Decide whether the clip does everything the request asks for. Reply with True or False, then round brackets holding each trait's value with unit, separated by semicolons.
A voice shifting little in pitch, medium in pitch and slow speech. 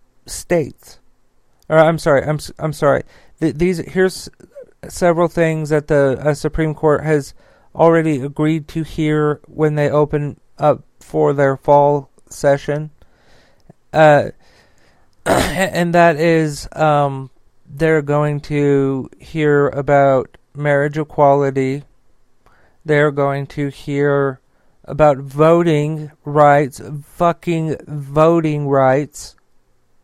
True (1.9 semitones; 150 Hz; 105 wpm)